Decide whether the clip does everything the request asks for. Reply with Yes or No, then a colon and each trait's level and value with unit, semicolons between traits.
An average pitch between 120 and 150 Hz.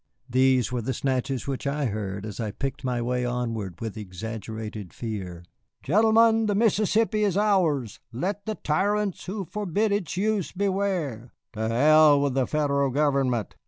Yes: medium, 140 Hz